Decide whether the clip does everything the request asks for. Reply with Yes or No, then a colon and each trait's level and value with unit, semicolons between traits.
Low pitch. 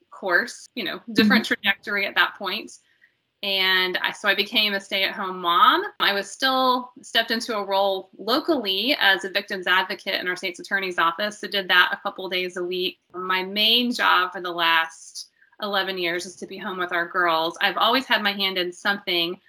No: high, 195 Hz